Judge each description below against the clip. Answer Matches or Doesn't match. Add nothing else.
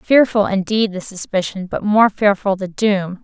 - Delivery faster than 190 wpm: Doesn't match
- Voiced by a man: Doesn't match